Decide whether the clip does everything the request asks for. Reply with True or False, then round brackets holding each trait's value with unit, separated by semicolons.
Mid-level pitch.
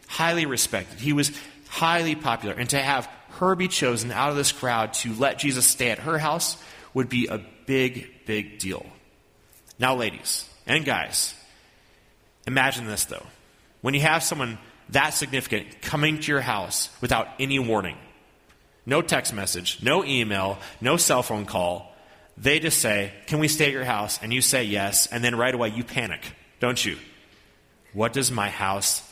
False (125 Hz)